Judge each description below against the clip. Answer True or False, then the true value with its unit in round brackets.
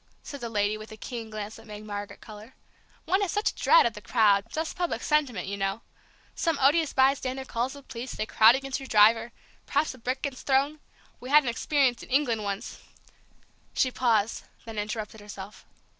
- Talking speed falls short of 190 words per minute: False (200 wpm)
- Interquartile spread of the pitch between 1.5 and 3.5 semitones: False (4.3 semitones)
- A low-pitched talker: False (235 Hz)